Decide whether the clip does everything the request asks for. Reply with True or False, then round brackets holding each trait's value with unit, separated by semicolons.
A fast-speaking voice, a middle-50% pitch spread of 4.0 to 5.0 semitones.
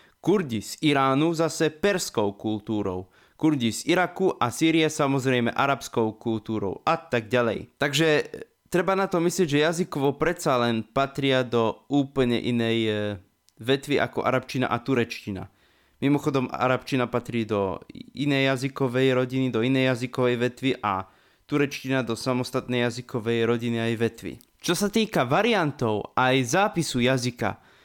False (135 wpm; 4.3 semitones)